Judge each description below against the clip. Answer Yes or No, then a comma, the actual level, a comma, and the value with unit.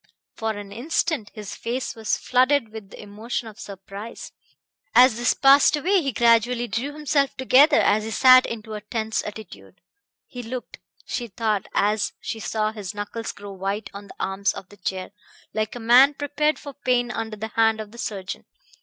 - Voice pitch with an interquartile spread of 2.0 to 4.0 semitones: Yes, average, 3.5 semitones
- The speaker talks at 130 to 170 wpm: No, average, 180 wpm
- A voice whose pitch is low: No, high, 225 Hz